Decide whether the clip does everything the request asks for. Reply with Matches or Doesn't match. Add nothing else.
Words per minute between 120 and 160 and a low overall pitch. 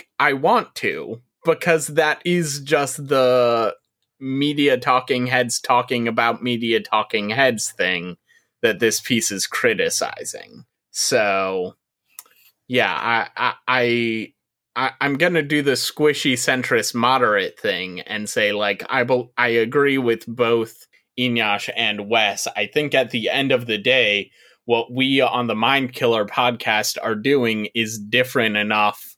Matches